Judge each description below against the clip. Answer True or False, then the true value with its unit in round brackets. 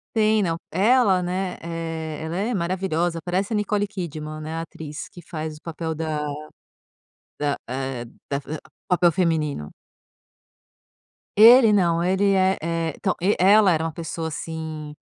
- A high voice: False (170 Hz)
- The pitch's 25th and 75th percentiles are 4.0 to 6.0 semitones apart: False (3.4 semitones)